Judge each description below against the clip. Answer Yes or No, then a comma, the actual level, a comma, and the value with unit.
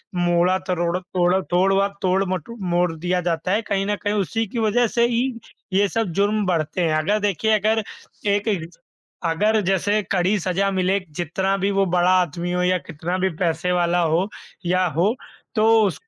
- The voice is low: No, medium, 185 Hz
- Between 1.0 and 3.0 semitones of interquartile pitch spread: Yes, narrow, 2.6 semitones